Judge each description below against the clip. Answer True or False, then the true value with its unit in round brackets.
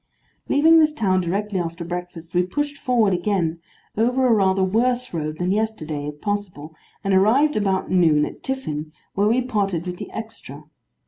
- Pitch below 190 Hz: False (195 Hz)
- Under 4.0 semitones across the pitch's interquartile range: False (5.0 semitones)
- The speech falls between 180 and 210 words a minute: False (170 wpm)